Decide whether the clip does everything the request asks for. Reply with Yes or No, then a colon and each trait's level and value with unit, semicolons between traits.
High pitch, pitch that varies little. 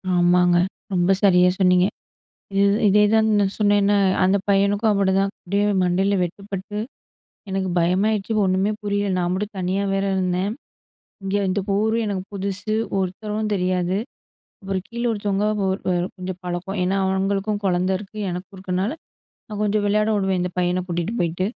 Yes: high, 195 Hz; narrow, 2.0 semitones